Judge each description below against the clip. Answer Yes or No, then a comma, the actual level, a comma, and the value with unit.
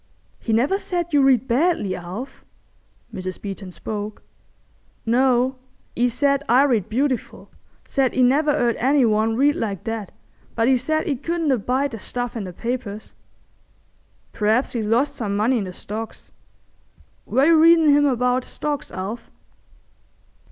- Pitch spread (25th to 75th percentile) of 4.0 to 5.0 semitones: Yes, average, 4.3 semitones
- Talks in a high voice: Yes, high, 245 Hz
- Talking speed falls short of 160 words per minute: Yes, average, 150 wpm